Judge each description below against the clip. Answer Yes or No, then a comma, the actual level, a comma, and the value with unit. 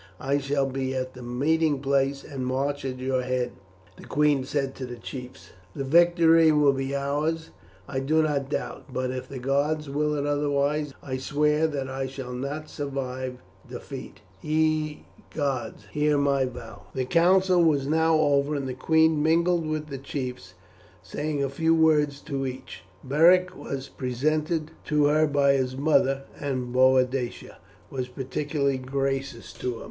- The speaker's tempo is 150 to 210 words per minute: Yes, average, 160 wpm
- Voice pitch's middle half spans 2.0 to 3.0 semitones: Yes, narrow, 2.6 semitones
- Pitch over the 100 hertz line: Yes, medium, 140 Hz